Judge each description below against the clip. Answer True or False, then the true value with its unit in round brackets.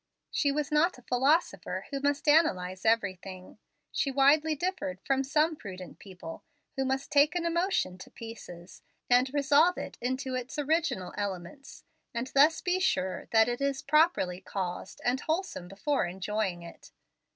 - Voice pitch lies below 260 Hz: False (265 Hz)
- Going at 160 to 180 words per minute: False (150 wpm)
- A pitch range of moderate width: False (7.8 semitones)